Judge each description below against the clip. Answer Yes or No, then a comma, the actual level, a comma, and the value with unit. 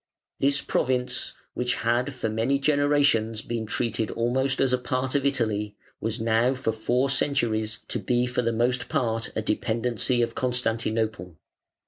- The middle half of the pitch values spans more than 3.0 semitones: No, narrow, 2.5 semitones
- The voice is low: Yes, low, 120 Hz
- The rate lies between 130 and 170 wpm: Yes, average, 150 wpm